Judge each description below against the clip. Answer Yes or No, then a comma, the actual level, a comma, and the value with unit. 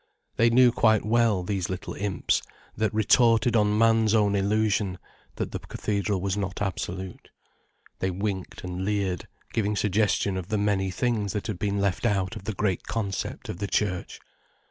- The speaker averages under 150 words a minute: No, average, 165 wpm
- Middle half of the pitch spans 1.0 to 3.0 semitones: Yes, narrow, 2.4 semitones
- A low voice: Yes, low, 100 Hz